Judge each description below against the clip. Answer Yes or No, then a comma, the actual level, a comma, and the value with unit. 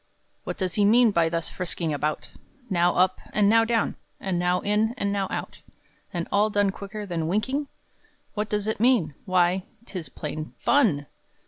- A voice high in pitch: Yes, high, 195 Hz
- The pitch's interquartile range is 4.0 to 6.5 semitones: No, average, 3.6 semitones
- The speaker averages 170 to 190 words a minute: Yes, average, 175 wpm